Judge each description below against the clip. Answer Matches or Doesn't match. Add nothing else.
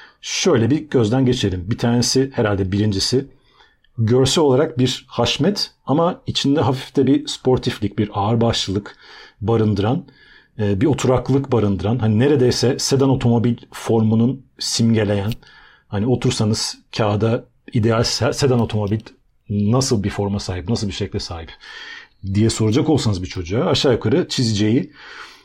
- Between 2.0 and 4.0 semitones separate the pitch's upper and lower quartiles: Matches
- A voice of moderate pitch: Doesn't match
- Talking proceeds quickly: Doesn't match